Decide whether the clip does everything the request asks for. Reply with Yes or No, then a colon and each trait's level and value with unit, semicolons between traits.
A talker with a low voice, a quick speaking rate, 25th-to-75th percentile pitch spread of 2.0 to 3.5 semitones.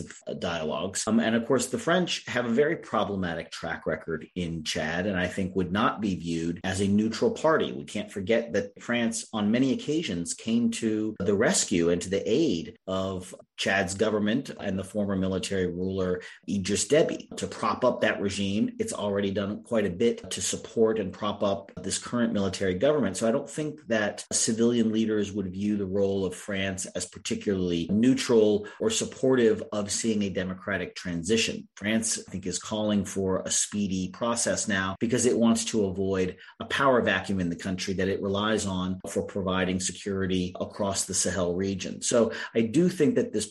No: low, 100 Hz; average, 185 wpm; average, 3.2 semitones